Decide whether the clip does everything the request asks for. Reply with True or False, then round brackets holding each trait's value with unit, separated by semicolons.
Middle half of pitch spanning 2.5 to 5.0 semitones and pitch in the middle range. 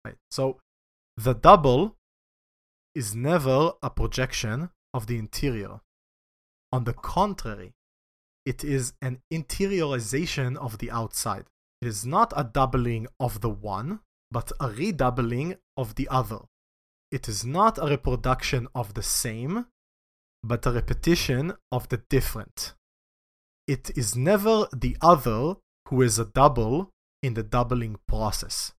False (3.7 semitones; 125 Hz)